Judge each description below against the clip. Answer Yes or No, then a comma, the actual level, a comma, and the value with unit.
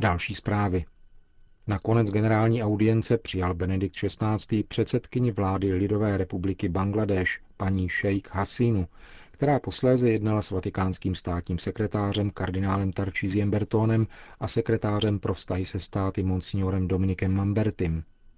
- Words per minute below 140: Yes, slow, 115 wpm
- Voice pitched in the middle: No, low, 100 Hz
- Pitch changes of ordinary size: No, narrow, 2.3 semitones